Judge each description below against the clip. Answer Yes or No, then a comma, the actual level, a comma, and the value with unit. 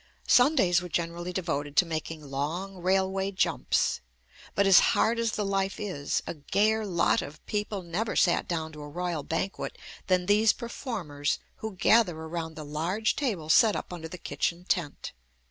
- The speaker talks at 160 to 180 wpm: Yes, average, 175 wpm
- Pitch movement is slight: No, average, 4.0 semitones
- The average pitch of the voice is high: No, medium, 180 Hz